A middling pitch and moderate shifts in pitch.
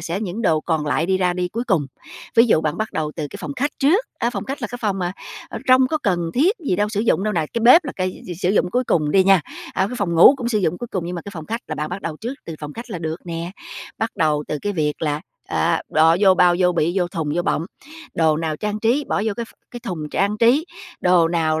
No: medium, 180 Hz; wide, 5.7 semitones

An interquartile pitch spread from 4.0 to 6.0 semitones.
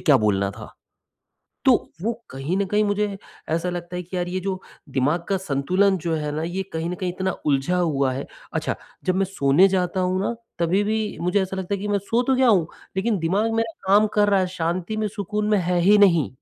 No: average, 3.3 semitones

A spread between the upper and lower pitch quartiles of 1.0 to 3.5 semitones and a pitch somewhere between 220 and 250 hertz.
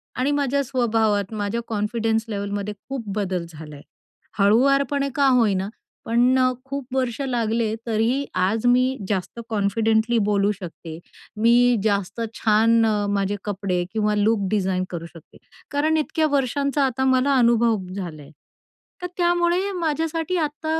No: average, 4.8 semitones; high, 230 Hz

